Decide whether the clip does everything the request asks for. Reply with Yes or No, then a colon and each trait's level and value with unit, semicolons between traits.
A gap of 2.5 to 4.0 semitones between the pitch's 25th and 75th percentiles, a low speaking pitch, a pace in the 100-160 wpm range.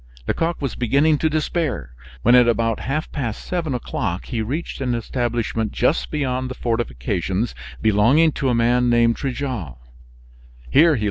Yes: average, 3.7 semitones; low, 125 Hz; average, 140 wpm